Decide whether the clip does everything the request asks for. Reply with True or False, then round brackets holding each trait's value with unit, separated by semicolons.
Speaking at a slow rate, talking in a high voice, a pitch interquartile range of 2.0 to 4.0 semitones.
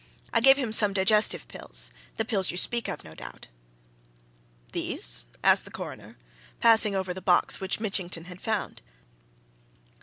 False (150 wpm; 195 Hz; 3.7 semitones)